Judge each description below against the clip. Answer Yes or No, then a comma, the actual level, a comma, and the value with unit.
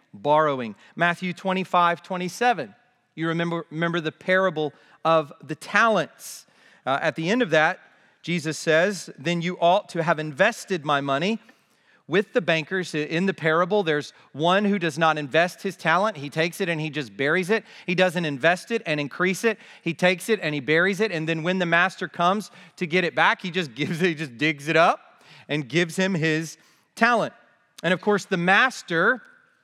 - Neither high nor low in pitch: Yes, medium, 175 Hz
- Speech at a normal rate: Yes, average, 185 wpm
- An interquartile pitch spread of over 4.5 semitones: No, average, 3.1 semitones